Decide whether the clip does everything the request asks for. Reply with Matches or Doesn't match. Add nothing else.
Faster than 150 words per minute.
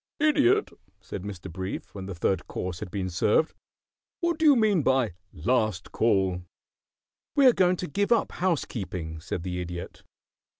Matches